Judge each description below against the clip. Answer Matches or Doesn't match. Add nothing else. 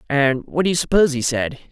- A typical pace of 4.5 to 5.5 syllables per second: Doesn't match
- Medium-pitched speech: Matches